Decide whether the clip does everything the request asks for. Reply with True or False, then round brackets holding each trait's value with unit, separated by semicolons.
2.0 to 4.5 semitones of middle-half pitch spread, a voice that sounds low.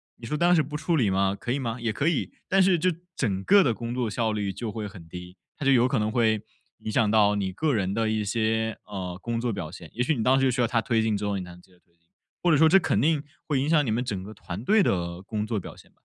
False (5.0 semitones; 110 Hz)